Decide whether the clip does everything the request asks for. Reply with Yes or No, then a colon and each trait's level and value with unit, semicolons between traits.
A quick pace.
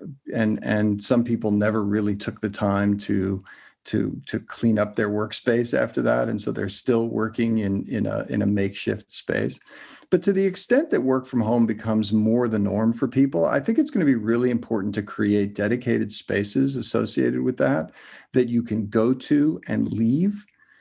No: average, 190 wpm